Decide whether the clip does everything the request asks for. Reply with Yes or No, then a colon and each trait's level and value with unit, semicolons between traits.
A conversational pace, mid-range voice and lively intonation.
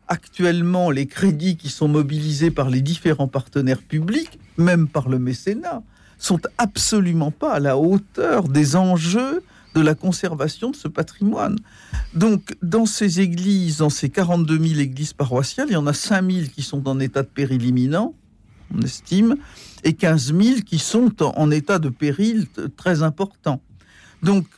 No: average, 160 wpm; medium, 165 Hz; average, 4.9 semitones